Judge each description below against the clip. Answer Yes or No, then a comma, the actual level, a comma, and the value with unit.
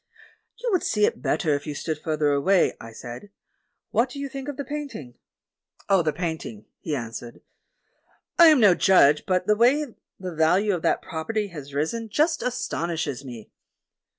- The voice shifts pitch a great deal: Yes, wide, 8.1 semitones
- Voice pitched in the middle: Yes, medium, 180 Hz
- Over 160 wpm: Yes, average, 180 wpm